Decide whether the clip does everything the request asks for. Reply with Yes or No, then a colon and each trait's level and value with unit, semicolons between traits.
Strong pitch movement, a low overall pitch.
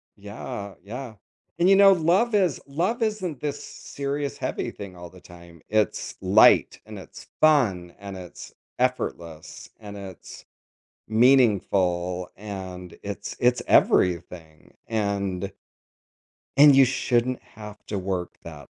Yes: wide, 7.1 semitones; low, 105 Hz